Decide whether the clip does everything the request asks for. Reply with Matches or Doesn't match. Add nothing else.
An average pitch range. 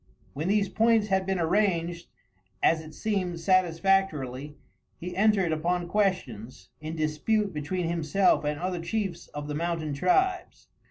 Matches